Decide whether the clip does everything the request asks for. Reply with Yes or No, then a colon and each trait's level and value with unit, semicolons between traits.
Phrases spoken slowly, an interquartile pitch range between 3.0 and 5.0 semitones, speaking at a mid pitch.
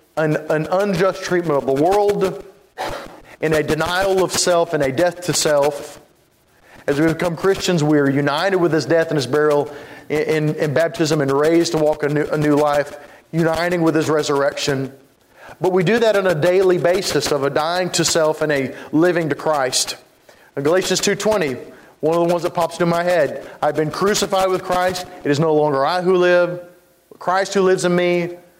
No: average, 195 wpm; average, 3.3 semitones; medium, 165 Hz